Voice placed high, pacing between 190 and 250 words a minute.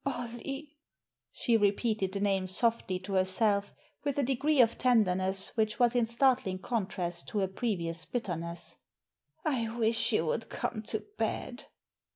No: high, 220 Hz; average, 150 wpm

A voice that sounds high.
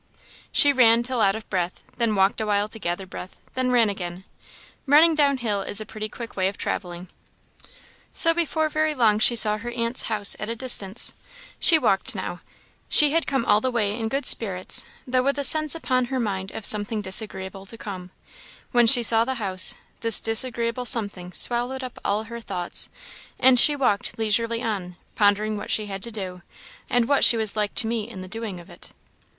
Yes: high, 225 Hz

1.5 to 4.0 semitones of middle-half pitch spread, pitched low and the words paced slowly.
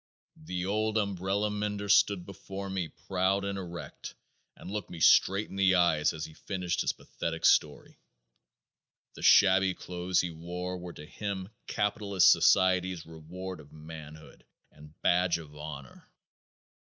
No: average, 3.1 semitones; very low, 90 Hz; average, 145 wpm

